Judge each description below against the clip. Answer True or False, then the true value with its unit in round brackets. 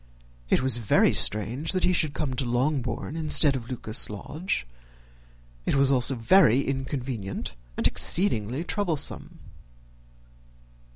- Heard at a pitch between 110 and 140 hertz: True (135 Hz)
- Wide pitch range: False (4.4 semitones)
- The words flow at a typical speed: False (125 wpm)